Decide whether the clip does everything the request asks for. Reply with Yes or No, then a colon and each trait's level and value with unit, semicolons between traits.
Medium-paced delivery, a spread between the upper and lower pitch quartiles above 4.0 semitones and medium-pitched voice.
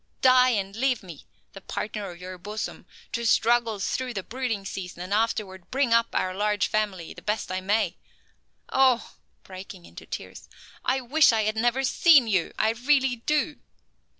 No: average, 170 wpm; average, 4.5 semitones; high, 220 Hz